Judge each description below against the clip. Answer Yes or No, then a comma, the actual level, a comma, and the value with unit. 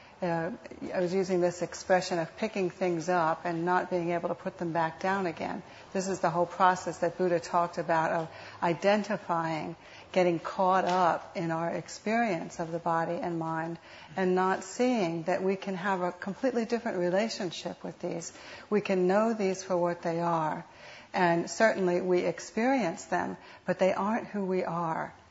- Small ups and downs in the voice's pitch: Yes, narrow, 2.0 semitones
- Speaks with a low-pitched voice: No, medium, 180 Hz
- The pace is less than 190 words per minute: Yes, average, 175 wpm